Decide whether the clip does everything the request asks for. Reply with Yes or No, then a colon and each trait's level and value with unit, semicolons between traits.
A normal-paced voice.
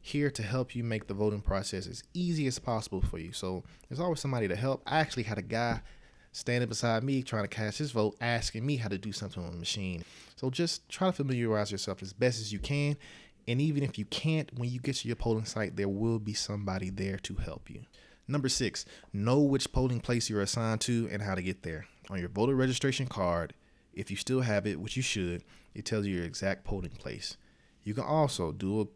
No: fast, 230 wpm